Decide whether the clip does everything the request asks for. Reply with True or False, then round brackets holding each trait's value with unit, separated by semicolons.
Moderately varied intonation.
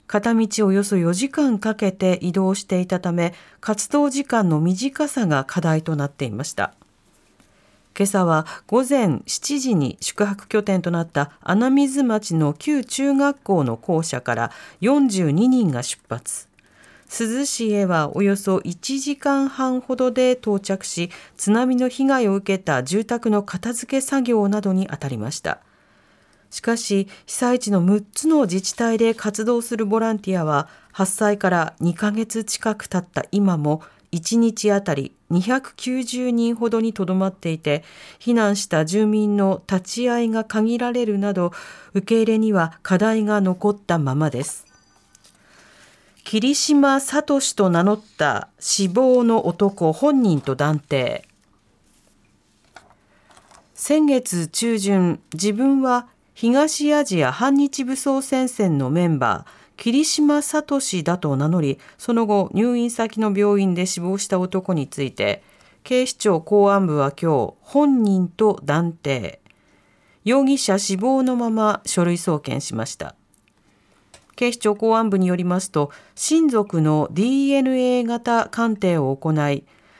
False (6.1 semitones)